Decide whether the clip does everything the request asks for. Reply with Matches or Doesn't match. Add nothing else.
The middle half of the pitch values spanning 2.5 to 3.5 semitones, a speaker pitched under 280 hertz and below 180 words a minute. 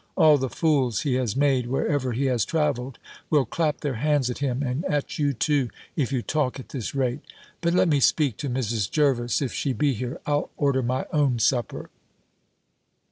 Doesn't match